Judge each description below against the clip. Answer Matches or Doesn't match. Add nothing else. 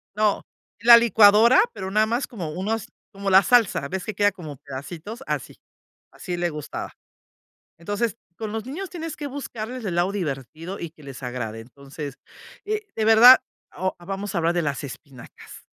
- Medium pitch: Doesn't match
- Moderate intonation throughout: Doesn't match